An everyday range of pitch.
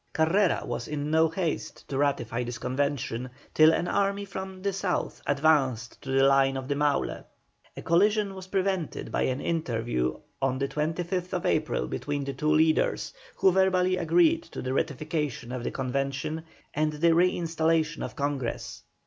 Yes: average, 4.6 semitones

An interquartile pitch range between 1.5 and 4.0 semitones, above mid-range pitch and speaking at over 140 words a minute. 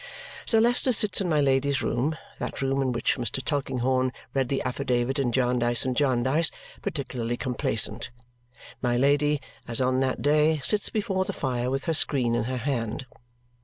No: average, 3.1 semitones; low, 130 Hz; average, 165 wpm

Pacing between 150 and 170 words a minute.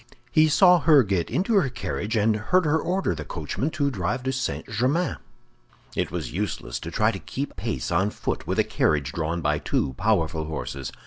No: average, 195 wpm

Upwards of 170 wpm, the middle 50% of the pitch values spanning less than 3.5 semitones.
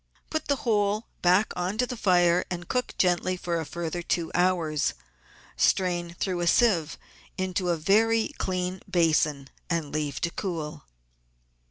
No: average, 150 wpm; narrow, 2.5 semitones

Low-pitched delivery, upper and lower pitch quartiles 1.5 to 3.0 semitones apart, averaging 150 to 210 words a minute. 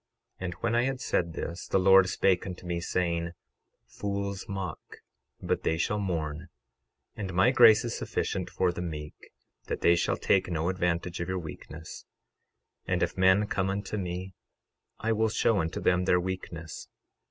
Yes: very low, 90 Hz; narrow, 2.5 semitones; average, 175 wpm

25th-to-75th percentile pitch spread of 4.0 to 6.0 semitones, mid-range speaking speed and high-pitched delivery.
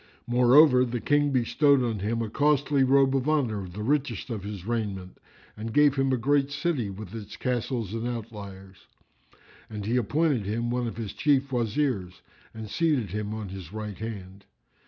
No: average, 4.5 semitones; average, 175 wpm; low, 115 Hz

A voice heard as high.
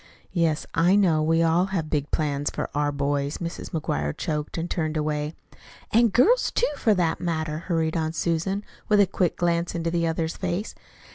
No: medium, 165 Hz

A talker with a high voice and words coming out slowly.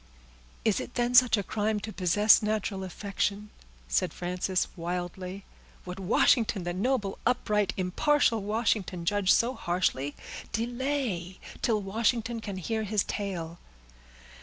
Yes: high, 205 Hz; slow, 120 wpm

